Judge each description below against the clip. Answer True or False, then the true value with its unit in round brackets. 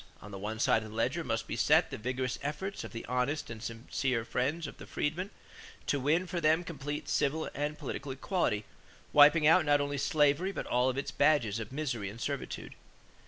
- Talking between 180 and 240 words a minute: True (200 wpm)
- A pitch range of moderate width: True (4.8 semitones)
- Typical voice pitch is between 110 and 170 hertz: True (140 Hz)